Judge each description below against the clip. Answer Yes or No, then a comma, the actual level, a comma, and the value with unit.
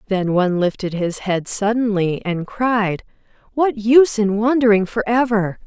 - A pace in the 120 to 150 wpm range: Yes, average, 140 wpm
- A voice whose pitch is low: No, high, 210 Hz